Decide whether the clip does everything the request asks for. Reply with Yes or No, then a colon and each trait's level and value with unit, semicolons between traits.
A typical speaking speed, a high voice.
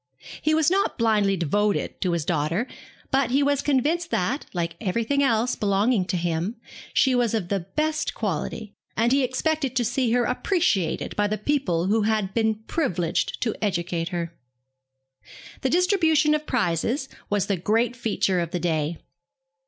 Yes: average, 165 wpm; high, 220 Hz